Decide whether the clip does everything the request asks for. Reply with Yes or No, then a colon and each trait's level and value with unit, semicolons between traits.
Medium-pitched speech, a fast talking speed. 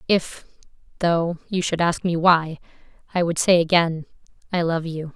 No: medium, 170 Hz; average, 165 wpm